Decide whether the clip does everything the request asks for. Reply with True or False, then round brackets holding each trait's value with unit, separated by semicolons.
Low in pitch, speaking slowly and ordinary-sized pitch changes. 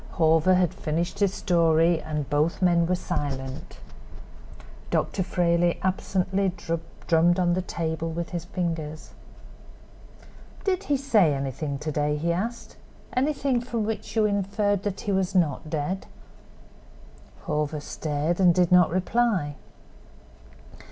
False (175 Hz; 125 wpm; 3.7 semitones)